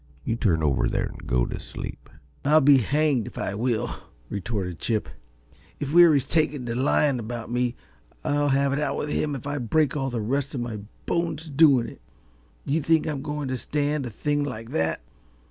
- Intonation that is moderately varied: Yes, average, 4.1 semitones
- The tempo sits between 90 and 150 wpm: No, average, 195 wpm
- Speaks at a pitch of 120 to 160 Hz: Yes, low, 135 Hz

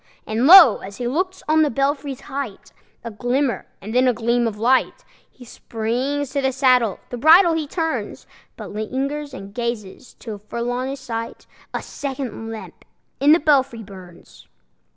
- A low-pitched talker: No, very high, 255 Hz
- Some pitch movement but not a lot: Yes, average, 3.8 semitones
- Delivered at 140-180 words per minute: Yes, average, 170 wpm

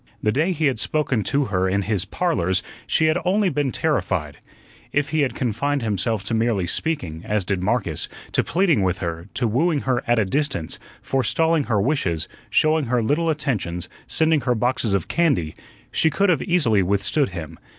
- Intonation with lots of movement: Yes, wide, 8.0 semitones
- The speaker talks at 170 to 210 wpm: Yes, average, 180 wpm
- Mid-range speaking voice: No, low, 120 Hz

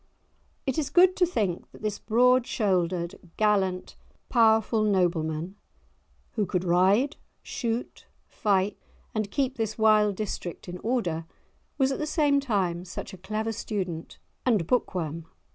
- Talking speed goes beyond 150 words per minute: No, average, 140 wpm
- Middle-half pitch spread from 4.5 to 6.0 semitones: Yes, average, 4.8 semitones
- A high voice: Yes, high, 210 Hz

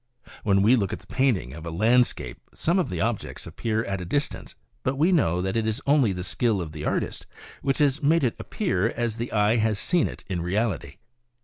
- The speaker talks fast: Yes, fast, 220 wpm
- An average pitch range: No, wide, 5.8 semitones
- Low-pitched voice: Yes, low, 110 Hz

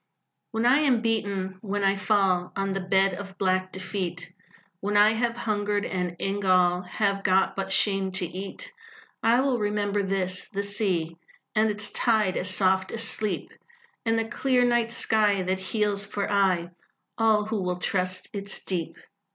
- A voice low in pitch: No, high, 200 Hz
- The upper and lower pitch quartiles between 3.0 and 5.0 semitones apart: No, narrow, 2.4 semitones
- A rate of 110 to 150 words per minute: No, average, 165 wpm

